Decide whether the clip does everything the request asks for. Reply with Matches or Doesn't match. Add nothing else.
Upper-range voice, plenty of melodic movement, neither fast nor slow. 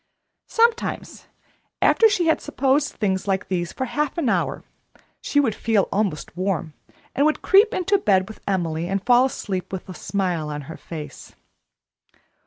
Matches